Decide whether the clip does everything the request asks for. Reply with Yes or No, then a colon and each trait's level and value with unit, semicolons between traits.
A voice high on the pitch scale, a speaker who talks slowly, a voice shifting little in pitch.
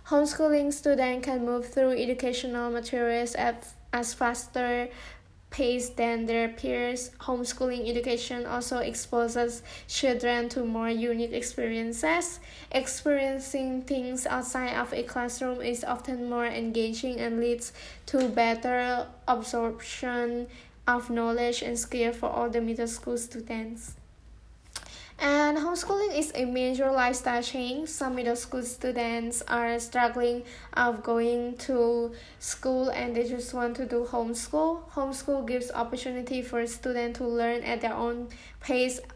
Yes: high, 245 Hz; slow, 125 wpm; narrow, 1.4 semitones